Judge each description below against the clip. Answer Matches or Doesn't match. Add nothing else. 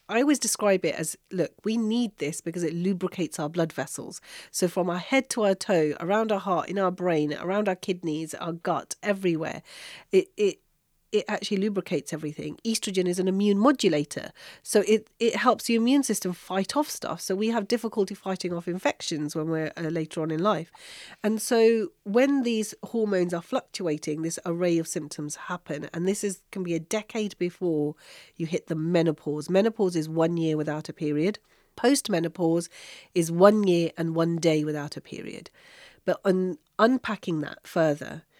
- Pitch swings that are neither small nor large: Matches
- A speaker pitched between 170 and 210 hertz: Matches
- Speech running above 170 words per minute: Matches